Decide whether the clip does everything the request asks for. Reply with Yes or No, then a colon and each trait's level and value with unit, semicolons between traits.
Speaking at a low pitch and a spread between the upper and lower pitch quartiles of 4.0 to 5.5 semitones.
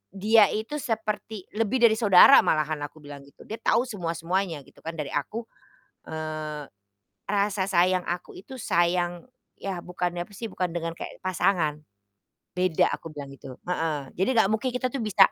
No: medium, 180 Hz; average, 4.9 semitones